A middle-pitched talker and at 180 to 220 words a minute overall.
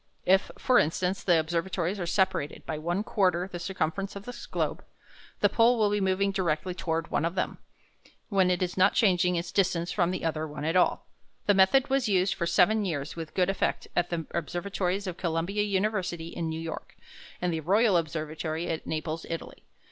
Yes: medium, 180 Hz; average, 195 wpm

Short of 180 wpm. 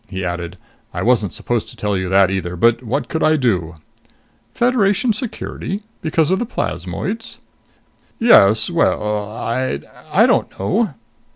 Yes: average, 145 wpm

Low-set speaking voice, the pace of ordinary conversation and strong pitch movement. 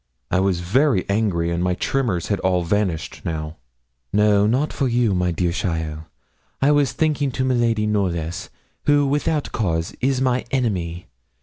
Yes: low, 105 Hz; average, 150 wpm; wide, 7.1 semitones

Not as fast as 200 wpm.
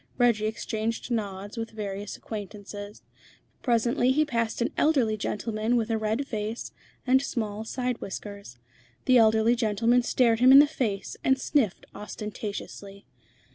Yes: slow, 135 wpm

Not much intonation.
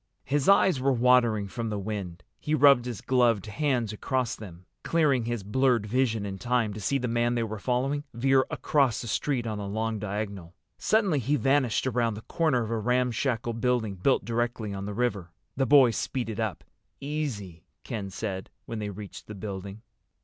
No: average, 3.8 semitones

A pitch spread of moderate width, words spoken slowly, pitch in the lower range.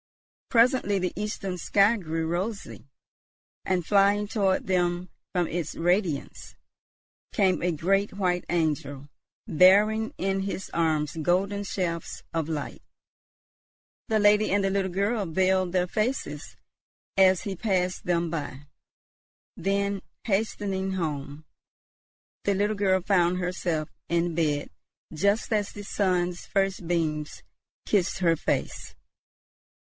No: average, 3.0 semitones; slow, 120 wpm; medium, 185 Hz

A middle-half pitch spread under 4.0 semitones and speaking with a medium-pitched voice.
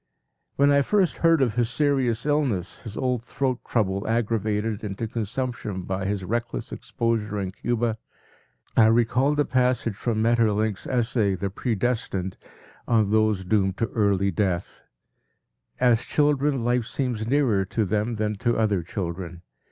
No: average, 3.6 semitones; low, 110 Hz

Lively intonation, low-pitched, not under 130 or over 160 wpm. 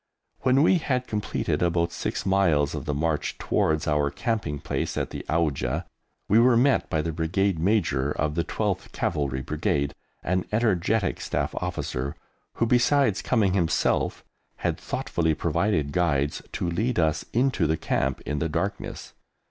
Yes: wide, 6.0 semitones; very low, 85 Hz; average, 155 wpm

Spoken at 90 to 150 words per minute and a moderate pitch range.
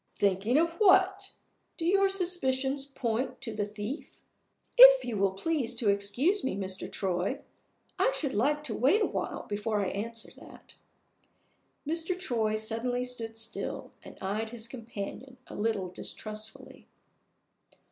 No: average, 140 wpm; wide, 5.9 semitones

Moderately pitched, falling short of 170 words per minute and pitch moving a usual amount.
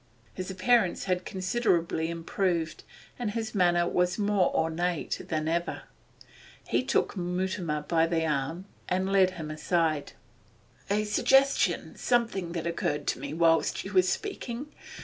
Yes: medium, 180 Hz; slow, 135 wpm; average, 3.3 semitones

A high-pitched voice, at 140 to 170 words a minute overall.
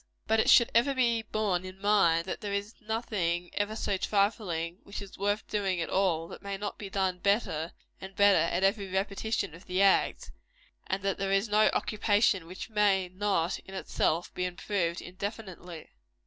No: high, 195 Hz; average, 180 wpm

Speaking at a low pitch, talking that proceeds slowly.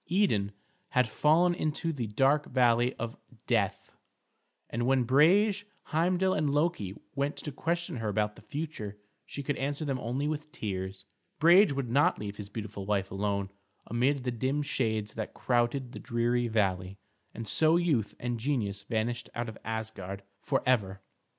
No: low, 120 Hz; average, 155 wpm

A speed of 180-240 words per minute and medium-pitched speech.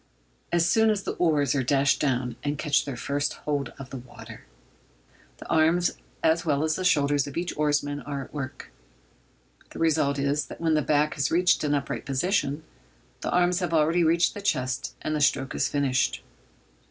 Yes: average, 190 wpm; medium, 145 Hz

